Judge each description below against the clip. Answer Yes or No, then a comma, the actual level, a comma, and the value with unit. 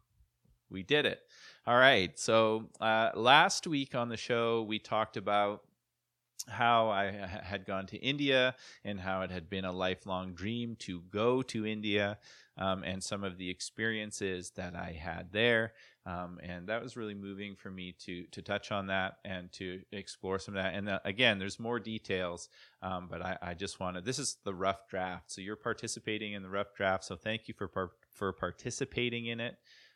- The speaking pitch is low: Yes, low, 100 Hz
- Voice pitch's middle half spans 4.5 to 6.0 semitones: No, average, 3.2 semitones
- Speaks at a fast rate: No, average, 190 wpm